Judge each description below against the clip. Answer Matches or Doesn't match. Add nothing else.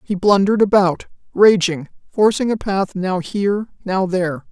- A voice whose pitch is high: Matches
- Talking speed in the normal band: Matches